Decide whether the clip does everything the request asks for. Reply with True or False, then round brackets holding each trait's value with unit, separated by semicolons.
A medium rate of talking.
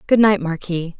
True (180 wpm)